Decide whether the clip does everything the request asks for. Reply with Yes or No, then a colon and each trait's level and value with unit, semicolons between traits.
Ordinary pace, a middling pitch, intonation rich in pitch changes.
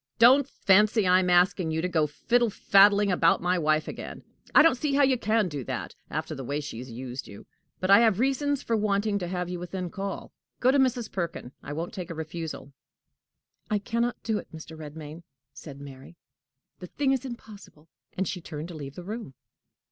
No: fast, 210 wpm; medium, 180 Hz; wide, 5.8 semitones